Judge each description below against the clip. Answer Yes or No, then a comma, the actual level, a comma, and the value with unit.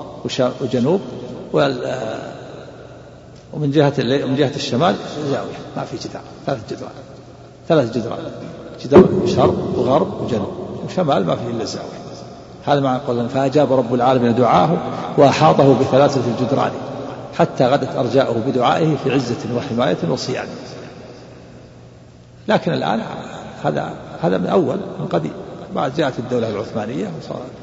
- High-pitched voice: No, low, 135 Hz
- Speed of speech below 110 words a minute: No, average, 120 wpm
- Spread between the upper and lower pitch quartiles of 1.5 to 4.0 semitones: Yes, narrow, 2.4 semitones